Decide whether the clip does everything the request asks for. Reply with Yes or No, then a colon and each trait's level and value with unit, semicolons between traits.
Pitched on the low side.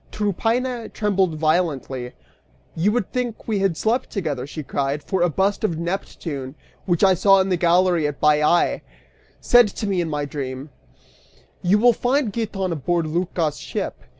No: medium, 180 Hz